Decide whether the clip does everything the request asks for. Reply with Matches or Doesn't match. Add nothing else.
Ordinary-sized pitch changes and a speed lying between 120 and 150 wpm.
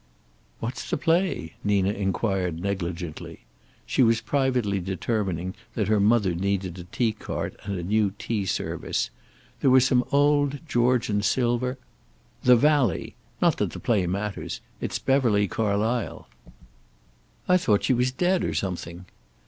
Matches